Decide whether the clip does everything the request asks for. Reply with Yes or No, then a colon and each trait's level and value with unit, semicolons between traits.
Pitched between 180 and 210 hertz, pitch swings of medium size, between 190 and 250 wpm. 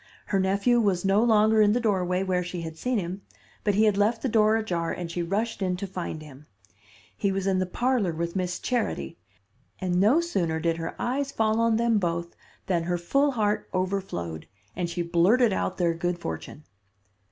Yes: high, 190 Hz; average, 4.2 semitones; average, 200 wpm